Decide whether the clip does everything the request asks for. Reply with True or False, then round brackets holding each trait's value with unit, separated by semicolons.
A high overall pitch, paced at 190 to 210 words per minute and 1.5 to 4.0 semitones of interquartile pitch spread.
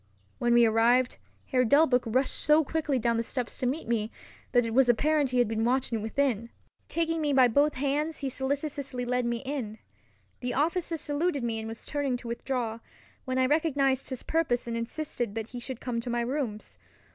True (255 Hz; 195 wpm; 3.4 semitones)